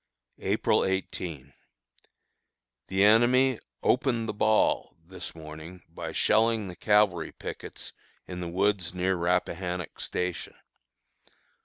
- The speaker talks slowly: Yes, slow, 105 wpm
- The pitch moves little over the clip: No, average, 3.5 semitones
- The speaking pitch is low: Yes, very low, 95 Hz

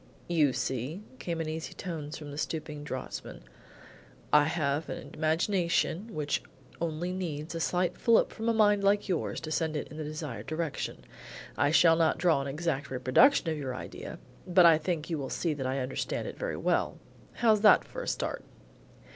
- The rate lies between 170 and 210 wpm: Yes, average, 185 wpm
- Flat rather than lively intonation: No, average, 3.3 semitones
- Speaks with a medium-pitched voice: Yes, medium, 160 Hz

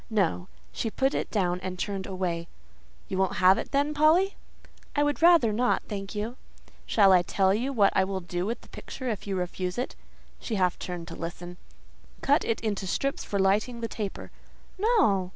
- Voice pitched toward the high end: Yes, high, 200 Hz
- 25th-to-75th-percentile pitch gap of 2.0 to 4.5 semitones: No, average, 5.1 semitones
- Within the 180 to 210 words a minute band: Yes, average, 190 wpm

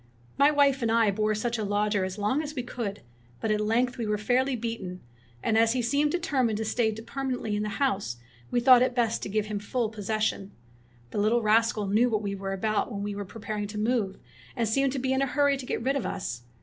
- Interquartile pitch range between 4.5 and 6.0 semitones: No, average, 3.3 semitones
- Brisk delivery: Yes, fast, 245 wpm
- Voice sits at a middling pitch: No, high, 225 Hz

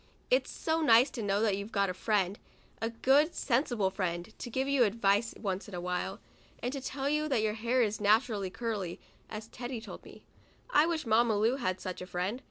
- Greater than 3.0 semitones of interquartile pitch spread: Yes, average, 4.4 semitones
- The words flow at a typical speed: No, fast, 215 wpm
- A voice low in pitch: No, high, 225 Hz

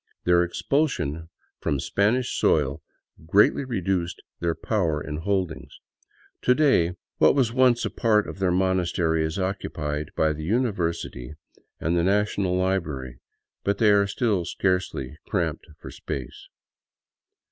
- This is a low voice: Yes, very low, 90 Hz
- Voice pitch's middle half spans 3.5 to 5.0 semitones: Yes, average, 4.2 semitones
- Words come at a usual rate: No, slow, 130 wpm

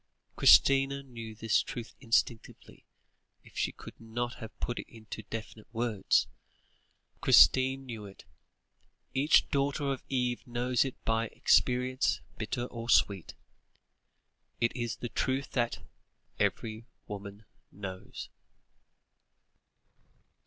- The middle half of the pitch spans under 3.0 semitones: Yes, narrow, 2.6 semitones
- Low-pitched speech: Yes, low, 120 Hz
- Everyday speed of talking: No, slow, 110 wpm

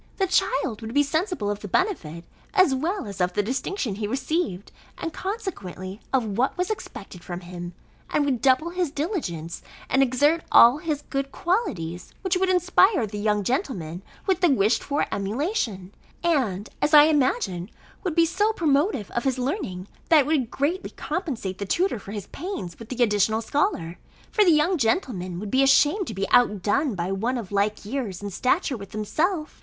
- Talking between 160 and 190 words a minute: Yes, average, 180 wpm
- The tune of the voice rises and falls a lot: Yes, wide, 8.4 semitones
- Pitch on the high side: Yes, very high, 260 Hz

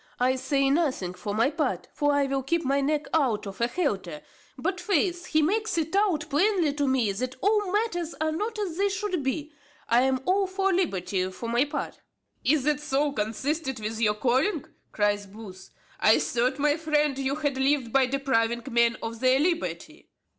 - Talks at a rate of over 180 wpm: Yes, average, 190 wpm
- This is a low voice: No, very high, 280 Hz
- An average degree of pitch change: No, wide, 5.7 semitones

